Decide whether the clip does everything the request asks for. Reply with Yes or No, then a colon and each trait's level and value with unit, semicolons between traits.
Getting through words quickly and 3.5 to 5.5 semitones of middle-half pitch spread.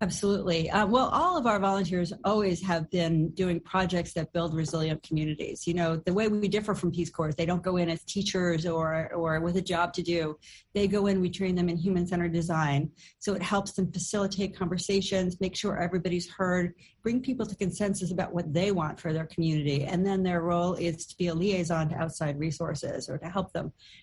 No: fast, 210 wpm; average, 2.7 semitones